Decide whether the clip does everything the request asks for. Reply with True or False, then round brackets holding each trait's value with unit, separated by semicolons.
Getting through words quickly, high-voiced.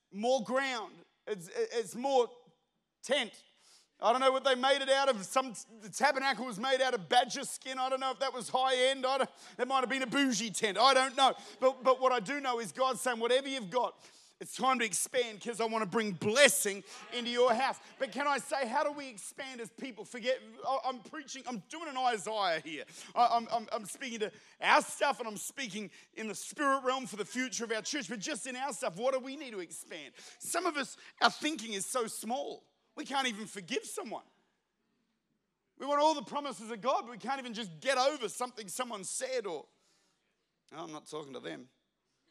True (220 wpm; 255 Hz)